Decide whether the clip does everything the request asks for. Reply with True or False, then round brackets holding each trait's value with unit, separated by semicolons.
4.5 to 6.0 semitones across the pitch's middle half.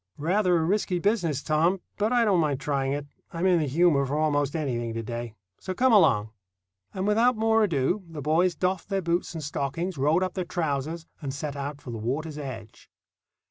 True (4.9 semitones)